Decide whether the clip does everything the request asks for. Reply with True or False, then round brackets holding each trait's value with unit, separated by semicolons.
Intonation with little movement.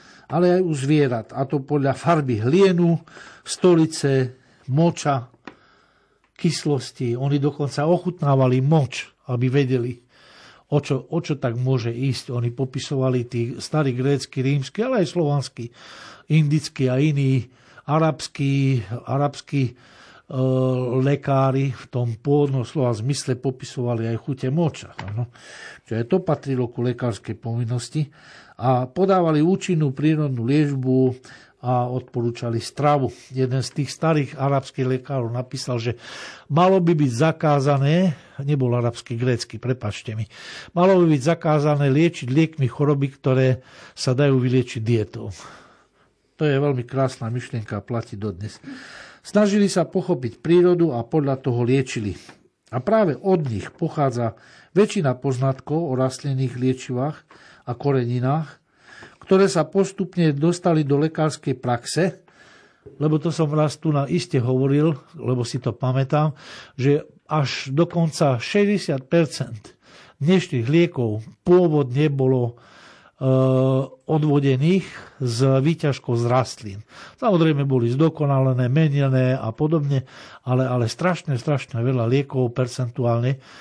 False (3.7 semitones)